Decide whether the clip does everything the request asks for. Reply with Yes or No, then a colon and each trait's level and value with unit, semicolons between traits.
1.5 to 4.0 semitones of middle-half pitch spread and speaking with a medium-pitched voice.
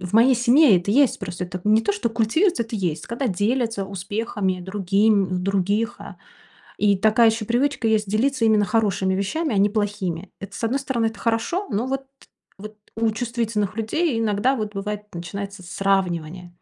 No: average, 2.9 semitones; high, 210 Hz